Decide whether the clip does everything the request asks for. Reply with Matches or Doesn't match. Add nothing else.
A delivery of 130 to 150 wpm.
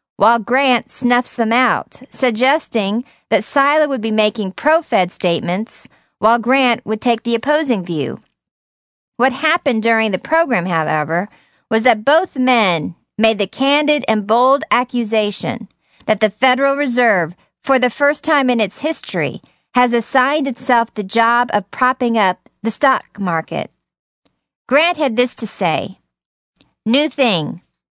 Matches